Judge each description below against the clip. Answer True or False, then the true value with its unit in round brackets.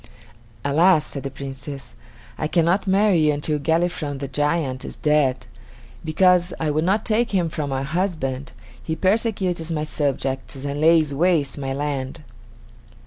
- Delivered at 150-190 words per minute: False (140 wpm)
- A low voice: False (155 Hz)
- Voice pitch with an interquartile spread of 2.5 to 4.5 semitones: True (3.9 semitones)